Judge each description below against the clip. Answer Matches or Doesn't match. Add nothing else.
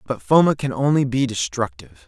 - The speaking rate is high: Doesn't match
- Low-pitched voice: Matches